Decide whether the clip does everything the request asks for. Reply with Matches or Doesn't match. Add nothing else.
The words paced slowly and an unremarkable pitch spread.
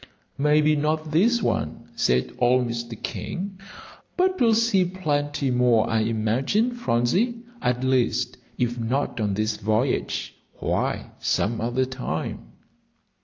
Doesn't match